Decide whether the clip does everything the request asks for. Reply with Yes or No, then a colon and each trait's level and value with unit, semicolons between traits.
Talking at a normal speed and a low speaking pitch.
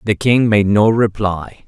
Yes: average, 180 wpm; low, 105 Hz